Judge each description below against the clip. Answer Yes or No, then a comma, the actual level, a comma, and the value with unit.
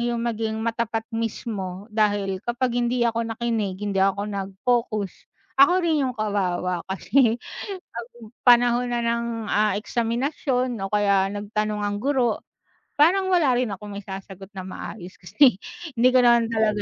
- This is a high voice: Yes, high, 225 Hz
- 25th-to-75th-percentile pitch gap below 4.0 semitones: Yes, average, 3.3 semitones